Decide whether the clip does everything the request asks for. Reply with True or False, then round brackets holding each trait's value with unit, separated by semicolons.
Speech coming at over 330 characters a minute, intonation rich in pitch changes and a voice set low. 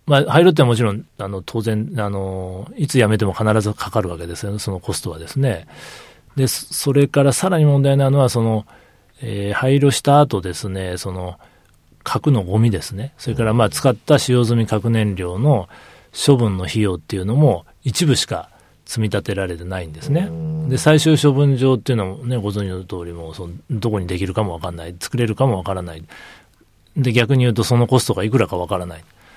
True (385 characters per minute; 5.8 semitones; 110 Hz)